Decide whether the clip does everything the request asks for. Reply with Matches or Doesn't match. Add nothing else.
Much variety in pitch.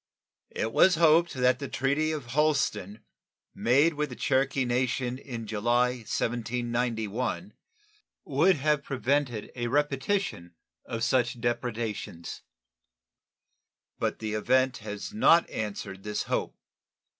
Doesn't match